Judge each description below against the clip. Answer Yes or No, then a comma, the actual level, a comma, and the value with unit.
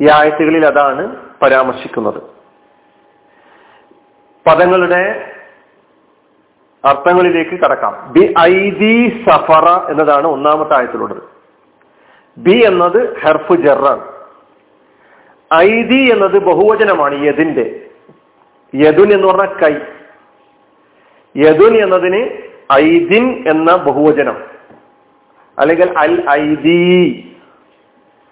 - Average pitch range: No, wide, 6.0 semitones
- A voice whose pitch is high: No, medium, 180 Hz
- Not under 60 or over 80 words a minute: Yes, average, 70 wpm